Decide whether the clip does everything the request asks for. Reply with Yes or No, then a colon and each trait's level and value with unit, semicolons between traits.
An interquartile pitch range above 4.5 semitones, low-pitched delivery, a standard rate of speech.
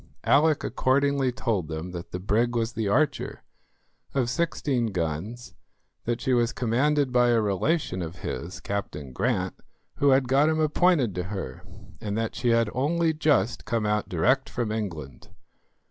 Yes: wide, 5.4 semitones; low, 120 Hz; average, 160 wpm